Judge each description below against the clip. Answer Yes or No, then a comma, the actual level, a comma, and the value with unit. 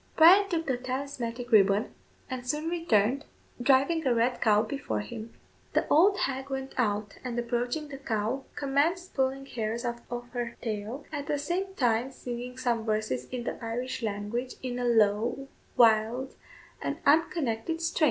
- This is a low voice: No, very high, 250 Hz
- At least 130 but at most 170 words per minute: Yes, average, 160 wpm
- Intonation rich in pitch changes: No, average, 3.6 semitones